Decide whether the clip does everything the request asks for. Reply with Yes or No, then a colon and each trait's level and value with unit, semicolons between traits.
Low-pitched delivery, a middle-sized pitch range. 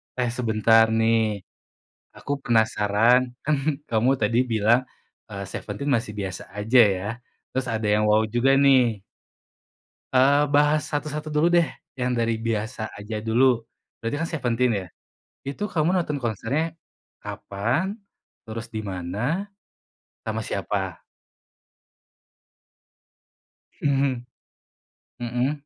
Yes: low, 120 Hz; average, 4.2 semitones